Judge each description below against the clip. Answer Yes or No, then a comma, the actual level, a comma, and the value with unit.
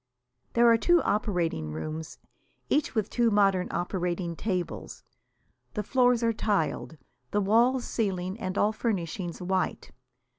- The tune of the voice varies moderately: Yes, average, 4.3 semitones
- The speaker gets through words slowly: Yes, slow, 125 wpm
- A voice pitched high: Yes, high, 200 Hz